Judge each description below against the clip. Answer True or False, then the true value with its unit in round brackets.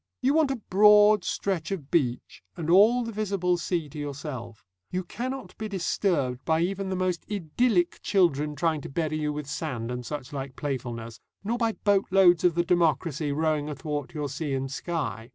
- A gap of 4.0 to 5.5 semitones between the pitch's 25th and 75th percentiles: True (5.2 semitones)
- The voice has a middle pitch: True (165 Hz)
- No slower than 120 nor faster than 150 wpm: False (175 wpm)